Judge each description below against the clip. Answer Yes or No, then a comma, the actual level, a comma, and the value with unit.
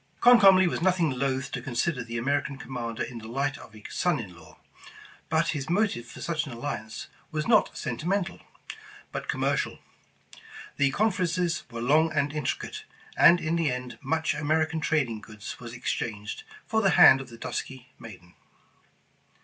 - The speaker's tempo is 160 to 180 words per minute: Yes, average, 165 wpm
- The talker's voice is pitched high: No, medium, 140 Hz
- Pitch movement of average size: No, wide, 5.8 semitones